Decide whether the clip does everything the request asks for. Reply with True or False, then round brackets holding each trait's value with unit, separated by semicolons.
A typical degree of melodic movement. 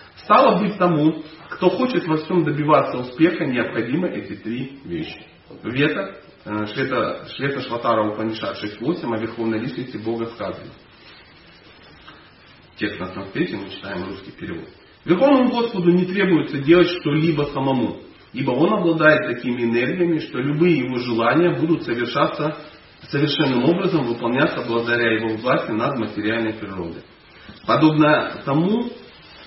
False (6.1 semitones)